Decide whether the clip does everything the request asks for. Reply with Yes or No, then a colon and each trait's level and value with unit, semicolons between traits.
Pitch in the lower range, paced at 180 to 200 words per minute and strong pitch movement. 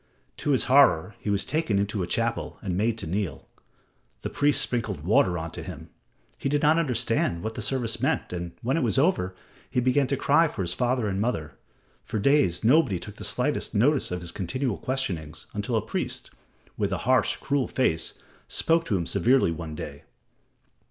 Yes: low, 110 Hz; average, 190 wpm; wide, 6.7 semitones